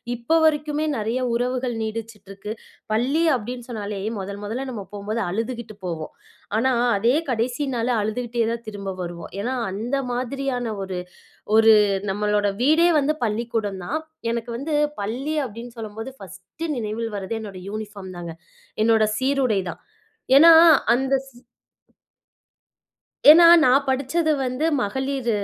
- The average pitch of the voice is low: No, high, 230 Hz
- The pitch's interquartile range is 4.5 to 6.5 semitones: No, average, 3.8 semitones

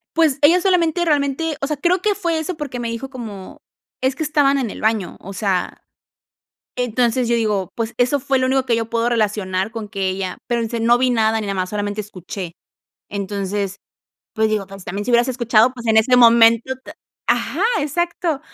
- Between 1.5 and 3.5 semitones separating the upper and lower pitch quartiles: No, average, 4.6 semitones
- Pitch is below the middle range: No, high, 235 Hz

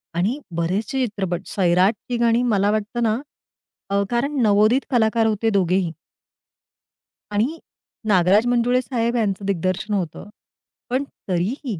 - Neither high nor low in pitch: No, high, 215 Hz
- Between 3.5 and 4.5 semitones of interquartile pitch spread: Yes, average, 3.8 semitones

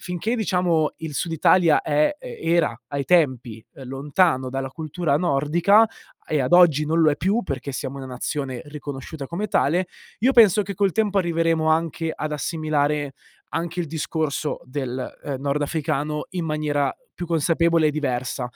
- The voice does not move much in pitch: No, average, 3.5 semitones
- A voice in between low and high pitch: Yes, medium, 155 Hz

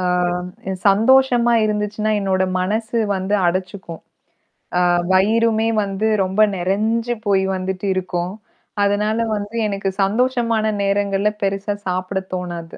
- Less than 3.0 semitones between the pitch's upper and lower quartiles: Yes, narrow, 2.5 semitones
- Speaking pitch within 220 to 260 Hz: No, high, 200 Hz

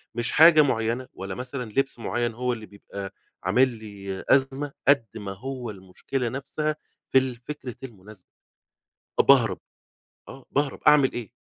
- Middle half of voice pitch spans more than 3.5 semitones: Yes, average, 4.1 semitones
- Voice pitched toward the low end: Yes, low, 125 Hz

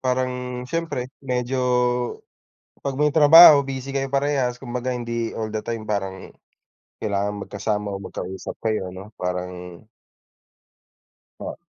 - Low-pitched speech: Yes, low, 120 Hz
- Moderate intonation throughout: Yes, average, 4.6 semitones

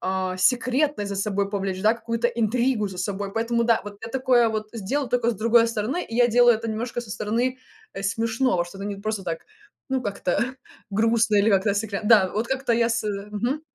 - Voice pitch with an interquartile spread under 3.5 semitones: Yes, average, 3.0 semitones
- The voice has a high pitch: Yes, high, 220 Hz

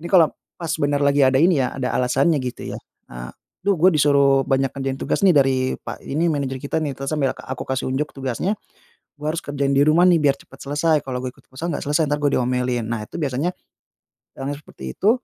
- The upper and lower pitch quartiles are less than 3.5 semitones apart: Yes, average, 2.7 semitones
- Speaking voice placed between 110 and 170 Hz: Yes, medium, 140 Hz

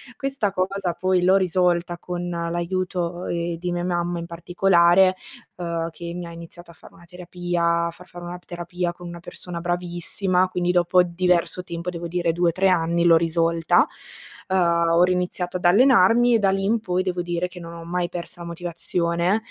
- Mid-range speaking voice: Yes, medium, 175 Hz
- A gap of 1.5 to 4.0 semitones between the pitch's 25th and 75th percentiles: No, narrow, 1.1 semitones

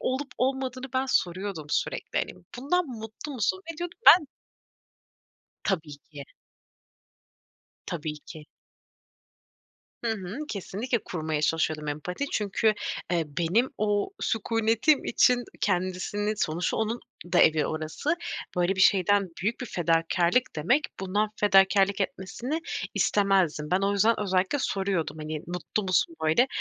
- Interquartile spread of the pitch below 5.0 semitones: No, wide, 5.4 semitones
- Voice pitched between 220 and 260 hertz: No, high, 195 Hz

